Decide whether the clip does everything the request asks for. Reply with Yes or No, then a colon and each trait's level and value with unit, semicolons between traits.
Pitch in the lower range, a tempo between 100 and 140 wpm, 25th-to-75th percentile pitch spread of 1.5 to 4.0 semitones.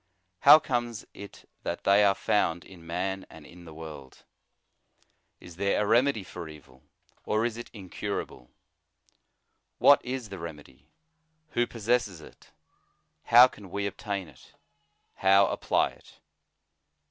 No: low, 100 Hz; slow, 135 wpm; average, 5.2 semitones